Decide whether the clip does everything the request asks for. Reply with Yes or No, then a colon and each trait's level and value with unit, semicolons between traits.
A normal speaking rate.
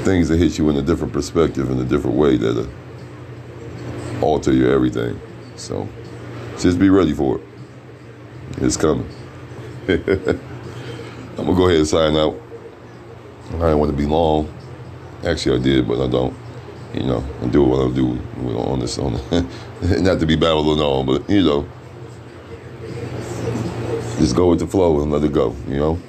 Yes: average, 170 wpm